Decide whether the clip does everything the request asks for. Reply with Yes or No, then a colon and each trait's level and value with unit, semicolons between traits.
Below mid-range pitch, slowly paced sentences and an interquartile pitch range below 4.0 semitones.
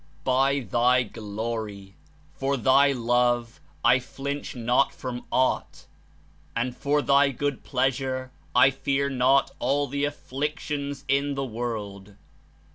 Yes: low, 130 Hz; slow, 120 wpm; narrow, 2.5 semitones